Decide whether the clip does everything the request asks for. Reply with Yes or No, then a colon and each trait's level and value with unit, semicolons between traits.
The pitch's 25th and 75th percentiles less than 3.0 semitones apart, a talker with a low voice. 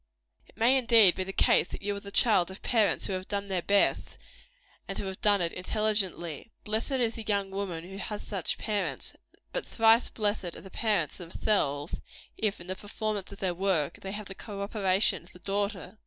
No: narrow, 2.4 semitones; high, 200 Hz